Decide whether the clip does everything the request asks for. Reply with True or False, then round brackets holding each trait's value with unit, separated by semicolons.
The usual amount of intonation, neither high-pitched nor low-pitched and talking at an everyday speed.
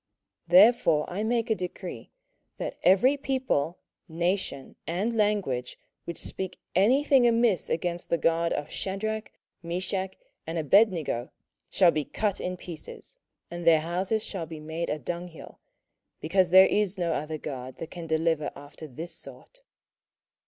True (4.2 semitones; 175 Hz; 145 wpm)